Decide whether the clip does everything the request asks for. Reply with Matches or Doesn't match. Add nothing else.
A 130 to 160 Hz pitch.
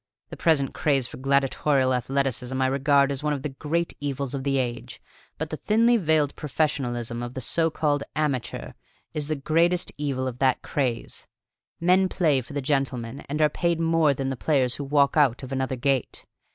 Matches